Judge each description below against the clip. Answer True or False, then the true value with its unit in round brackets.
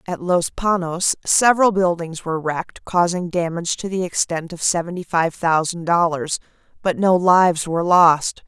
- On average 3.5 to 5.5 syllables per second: True (4.9 syllables/s)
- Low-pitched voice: False (175 Hz)